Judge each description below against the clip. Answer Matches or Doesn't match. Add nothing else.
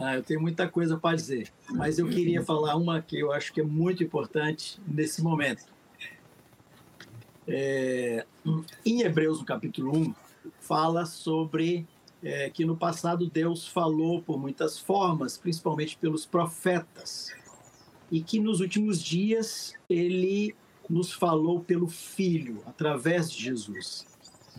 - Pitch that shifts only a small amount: Matches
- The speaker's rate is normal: Matches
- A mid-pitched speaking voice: Matches